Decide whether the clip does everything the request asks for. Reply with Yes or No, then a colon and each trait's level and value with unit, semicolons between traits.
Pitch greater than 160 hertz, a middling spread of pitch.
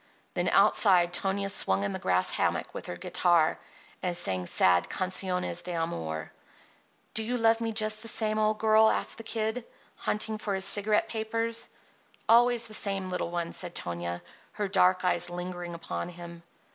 Yes: medium, 185 Hz; average, 4.1 semitones